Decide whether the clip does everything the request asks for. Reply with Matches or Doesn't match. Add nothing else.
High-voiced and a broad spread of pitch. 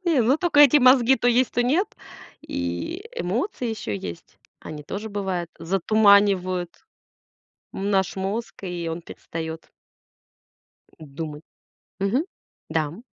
Matches